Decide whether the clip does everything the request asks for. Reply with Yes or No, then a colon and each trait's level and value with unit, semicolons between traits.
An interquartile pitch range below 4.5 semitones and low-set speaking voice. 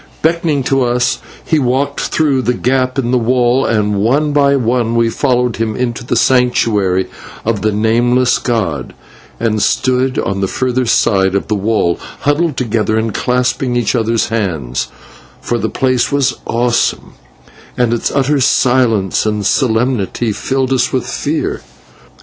Yes: average, 2.9 semitones; low, 120 Hz